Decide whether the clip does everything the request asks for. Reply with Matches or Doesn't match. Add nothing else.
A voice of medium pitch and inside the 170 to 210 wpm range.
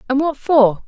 Doesn't match